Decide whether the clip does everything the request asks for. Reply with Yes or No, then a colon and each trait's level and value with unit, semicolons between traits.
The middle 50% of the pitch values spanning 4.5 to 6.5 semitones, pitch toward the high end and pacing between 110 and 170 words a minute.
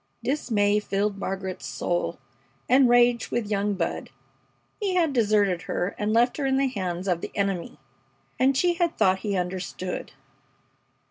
Yes: average, 5.0 semitones; high, 210 Hz; average, 150 wpm